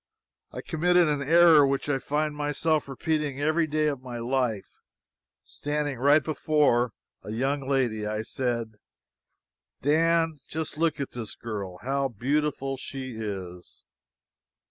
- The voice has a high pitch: No, medium, 140 Hz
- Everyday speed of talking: No, slow, 130 wpm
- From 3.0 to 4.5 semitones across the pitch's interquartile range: Yes, average, 4.0 semitones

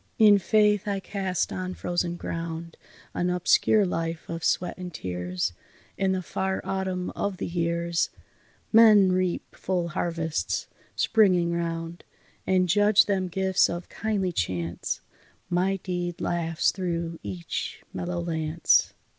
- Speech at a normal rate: No, slow, 130 wpm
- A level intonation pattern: Yes, narrow, 2.3 semitones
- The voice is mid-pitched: Yes, medium, 175 Hz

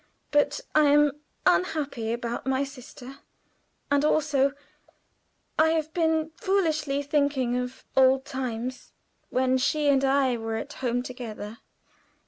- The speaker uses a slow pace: Yes, slow, 120 wpm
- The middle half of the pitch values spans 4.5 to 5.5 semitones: No, average, 2.8 semitones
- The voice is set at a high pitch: Yes, very high, 275 Hz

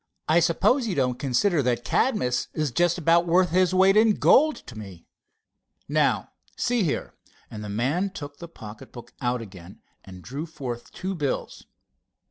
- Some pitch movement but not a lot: No, wide, 7.3 semitones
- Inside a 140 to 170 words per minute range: Yes, average, 165 wpm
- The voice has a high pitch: No, medium, 150 Hz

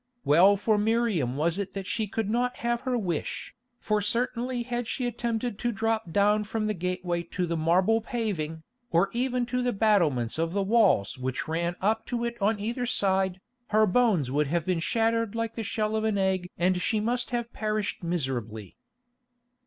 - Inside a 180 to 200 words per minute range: Yes, average, 190 wpm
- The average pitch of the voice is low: No, high, 210 Hz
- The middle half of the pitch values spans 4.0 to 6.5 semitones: Yes, average, 4.7 semitones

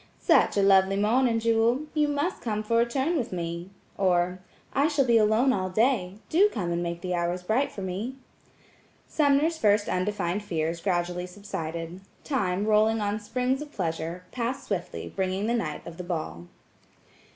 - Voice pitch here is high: Yes, high, 205 Hz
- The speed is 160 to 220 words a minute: Yes, average, 170 wpm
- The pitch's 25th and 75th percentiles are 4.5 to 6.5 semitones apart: Yes, average, 5.1 semitones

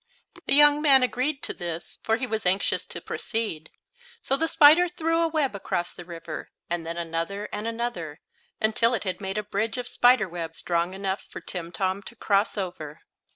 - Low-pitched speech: No, high, 205 Hz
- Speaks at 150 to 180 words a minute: No, average, 190 wpm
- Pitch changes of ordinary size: No, wide, 6.4 semitones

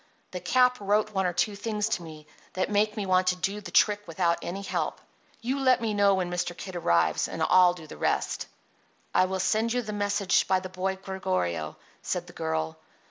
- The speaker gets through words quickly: Yes, fast, 210 wpm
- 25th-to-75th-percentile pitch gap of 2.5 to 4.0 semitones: Yes, average, 2.9 semitones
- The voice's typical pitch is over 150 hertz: Yes, high, 190 Hz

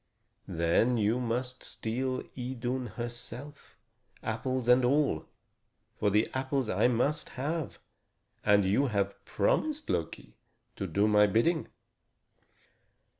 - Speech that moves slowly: Yes, slow, 110 wpm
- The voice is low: Yes, low, 120 Hz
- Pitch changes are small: No, average, 3.8 semitones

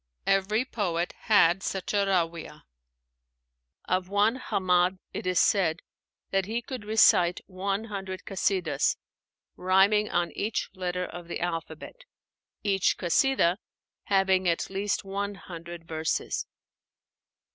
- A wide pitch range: No, narrow, 2.5 semitones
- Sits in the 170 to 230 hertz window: Yes, high, 190 Hz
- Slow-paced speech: Yes, slow, 115 wpm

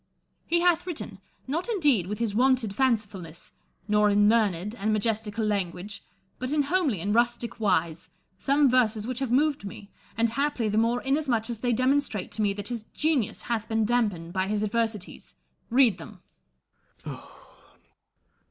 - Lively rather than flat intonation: No, average, 4.0 semitones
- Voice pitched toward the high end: Yes, high, 225 Hz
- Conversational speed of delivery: Yes, average, 155 wpm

